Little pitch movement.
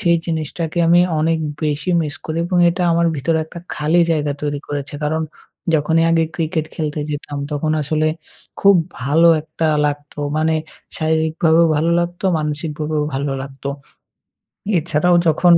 Yes: narrow, 2.0 semitones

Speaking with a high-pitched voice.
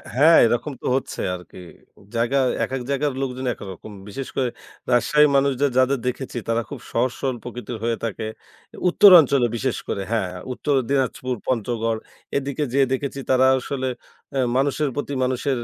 No: low, 130 Hz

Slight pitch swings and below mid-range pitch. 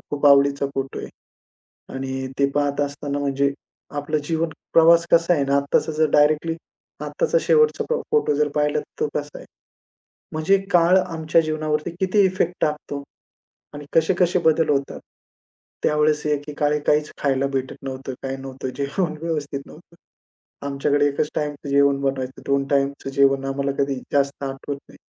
No: narrow, 2.2 semitones; medium, 145 Hz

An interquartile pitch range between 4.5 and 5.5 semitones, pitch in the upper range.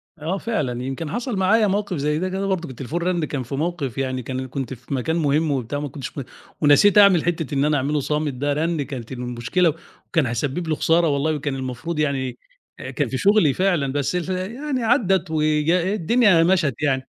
No: average, 5.0 semitones; medium, 155 Hz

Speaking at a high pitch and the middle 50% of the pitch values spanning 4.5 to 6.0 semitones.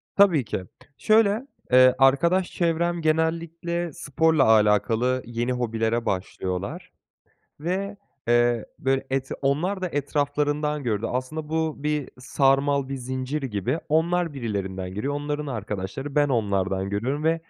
No: low, 135 Hz; average, 5.2 semitones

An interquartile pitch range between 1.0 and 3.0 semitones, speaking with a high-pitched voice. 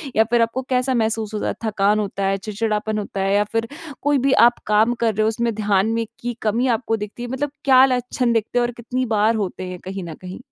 Yes: narrow, 2.6 semitones; high, 225 Hz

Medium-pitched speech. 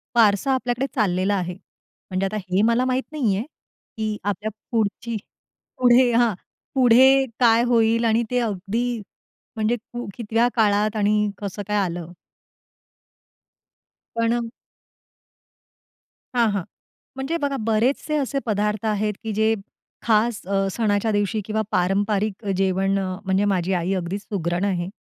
No: high, 215 Hz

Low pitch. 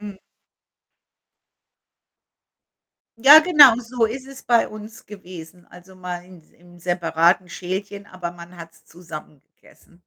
No: medium, 185 Hz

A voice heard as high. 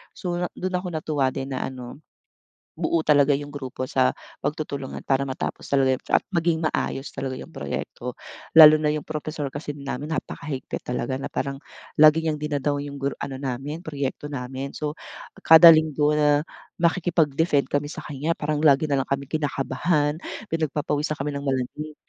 No: medium, 145 Hz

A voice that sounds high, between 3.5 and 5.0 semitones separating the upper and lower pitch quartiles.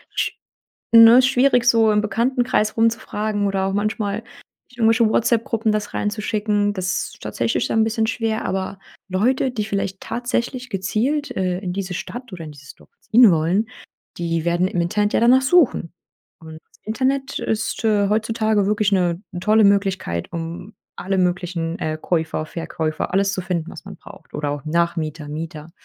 Yes: high, 205 Hz; average, 4.5 semitones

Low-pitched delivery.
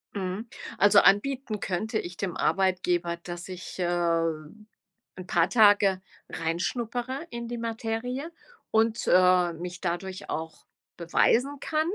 No: high, 190 Hz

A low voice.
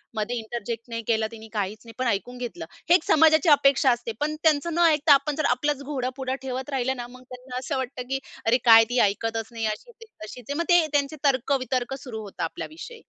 No: very high, 255 Hz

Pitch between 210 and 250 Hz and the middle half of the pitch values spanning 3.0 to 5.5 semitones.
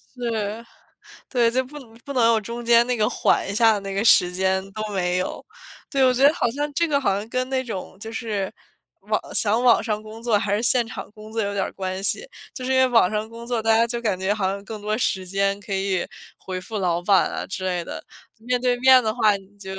Yes: high, 220 Hz; average, 3.5 semitones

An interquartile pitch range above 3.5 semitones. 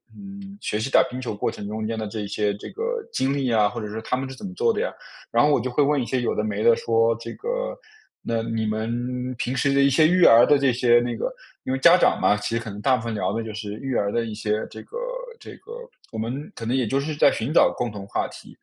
Yes: average, 4.1 semitones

